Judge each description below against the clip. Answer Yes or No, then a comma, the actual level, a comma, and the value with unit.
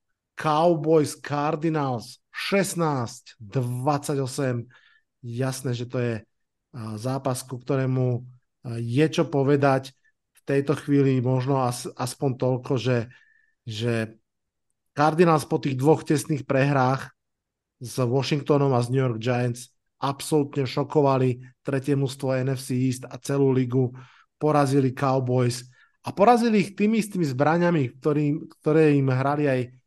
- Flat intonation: No, average, 3.0 semitones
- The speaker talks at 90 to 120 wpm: Yes, average, 115 wpm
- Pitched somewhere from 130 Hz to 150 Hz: Yes, low, 135 Hz